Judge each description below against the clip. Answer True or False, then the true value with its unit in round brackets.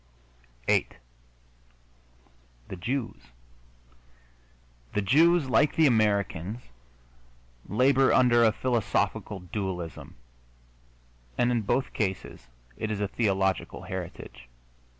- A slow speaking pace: True (90 wpm)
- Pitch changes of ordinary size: True (4.9 semitones)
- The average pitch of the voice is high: False (110 Hz)